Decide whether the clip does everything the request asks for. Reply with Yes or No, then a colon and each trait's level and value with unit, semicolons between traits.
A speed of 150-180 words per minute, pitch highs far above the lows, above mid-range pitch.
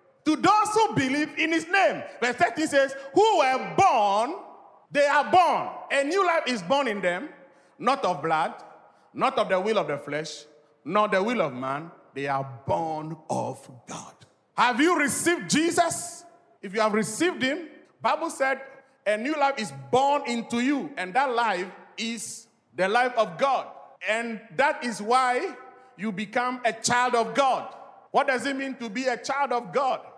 Yes: average, 175 wpm; wide, 5.9 semitones; very high, 260 Hz